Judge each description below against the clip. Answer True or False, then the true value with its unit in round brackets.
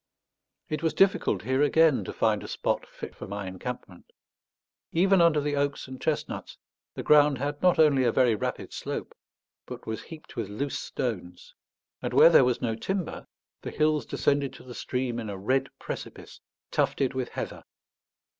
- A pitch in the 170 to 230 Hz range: False (135 Hz)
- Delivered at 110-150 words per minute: False (175 wpm)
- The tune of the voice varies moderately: True (4.7 semitones)